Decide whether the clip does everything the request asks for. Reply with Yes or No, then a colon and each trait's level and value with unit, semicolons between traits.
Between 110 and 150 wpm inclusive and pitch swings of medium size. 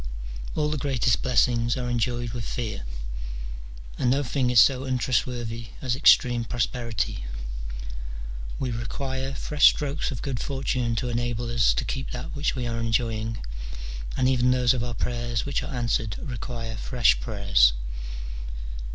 No: average, 145 wpm; narrow, 2.0 semitones